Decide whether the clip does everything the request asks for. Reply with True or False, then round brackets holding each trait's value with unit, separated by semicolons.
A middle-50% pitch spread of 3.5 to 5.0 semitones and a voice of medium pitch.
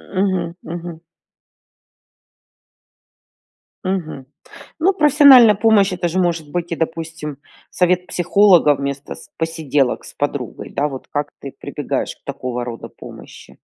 True (4.3 semitones; 170 Hz)